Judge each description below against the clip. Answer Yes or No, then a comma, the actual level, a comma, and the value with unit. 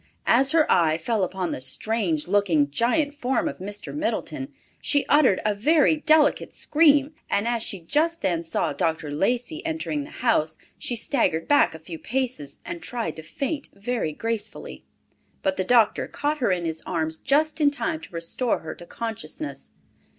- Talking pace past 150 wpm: Yes, average, 170 wpm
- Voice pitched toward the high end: Yes, high, 230 Hz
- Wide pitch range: Yes, wide, 9.0 semitones